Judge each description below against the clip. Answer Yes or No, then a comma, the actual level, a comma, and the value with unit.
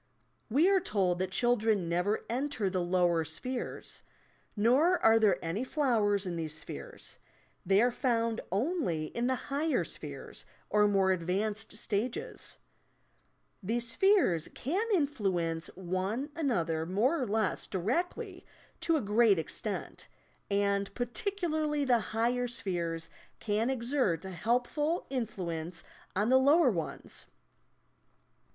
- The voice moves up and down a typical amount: No, wide, 5.9 semitones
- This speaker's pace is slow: Yes, slow, 125 wpm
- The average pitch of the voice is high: Yes, high, 220 Hz